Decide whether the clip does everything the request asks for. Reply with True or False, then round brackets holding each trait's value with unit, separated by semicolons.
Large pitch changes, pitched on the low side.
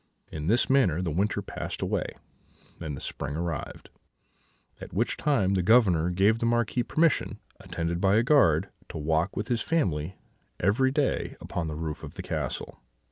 True (6.3 semitones; 95 Hz)